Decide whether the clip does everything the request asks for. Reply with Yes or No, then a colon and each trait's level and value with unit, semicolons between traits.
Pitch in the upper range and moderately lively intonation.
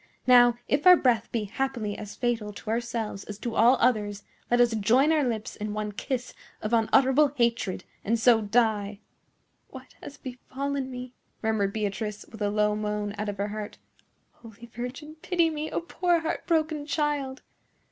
Yes: high, 235 Hz; average, 4.1 semitones